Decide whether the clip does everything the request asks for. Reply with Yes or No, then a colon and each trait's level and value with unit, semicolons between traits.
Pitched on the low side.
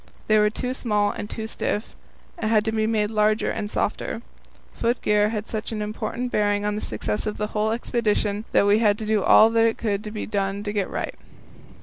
No: high, 215 Hz